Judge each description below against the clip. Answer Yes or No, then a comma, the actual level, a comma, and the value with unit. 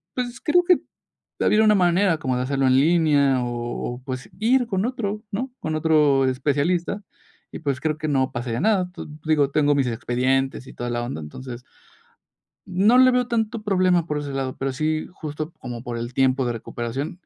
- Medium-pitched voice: Yes, medium, 150 Hz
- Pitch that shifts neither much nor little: No, wide, 6.5 semitones